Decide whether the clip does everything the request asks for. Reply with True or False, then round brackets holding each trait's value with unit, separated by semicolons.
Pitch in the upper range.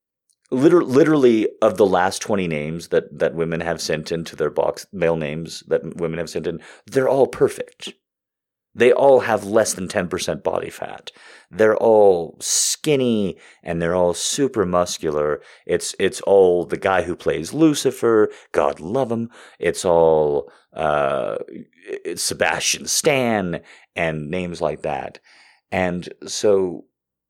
False (95 Hz)